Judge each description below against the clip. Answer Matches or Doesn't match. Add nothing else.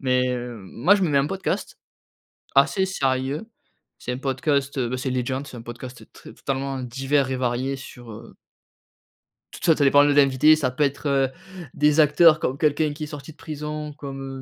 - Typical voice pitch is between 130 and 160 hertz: Matches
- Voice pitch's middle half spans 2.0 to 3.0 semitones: Matches